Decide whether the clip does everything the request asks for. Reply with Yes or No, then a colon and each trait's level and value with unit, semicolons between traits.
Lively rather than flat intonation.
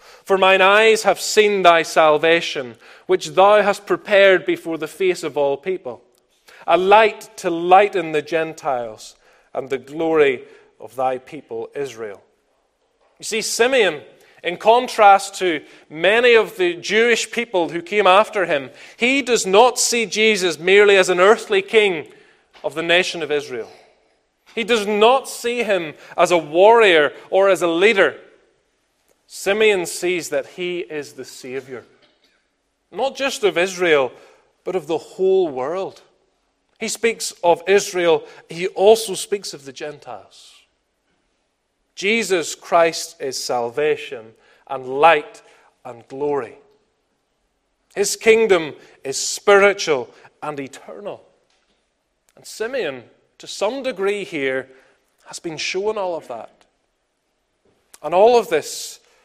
Yes: wide, 8.3 semitones